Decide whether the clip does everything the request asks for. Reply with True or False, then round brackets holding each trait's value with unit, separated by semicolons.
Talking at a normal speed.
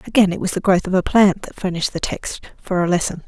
False (275 wpm)